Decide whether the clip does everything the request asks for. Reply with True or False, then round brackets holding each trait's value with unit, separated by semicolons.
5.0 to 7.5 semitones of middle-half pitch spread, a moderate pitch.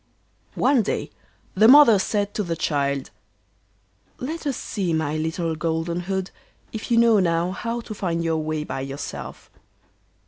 True (5.4 semitones; 175 Hz)